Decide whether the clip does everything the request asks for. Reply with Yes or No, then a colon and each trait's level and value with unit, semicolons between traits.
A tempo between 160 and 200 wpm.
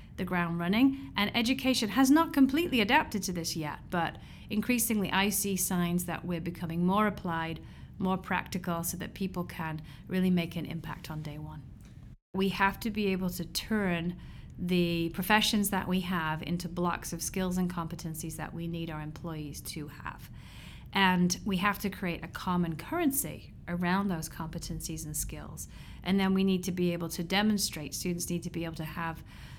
Yes: average, 180 wpm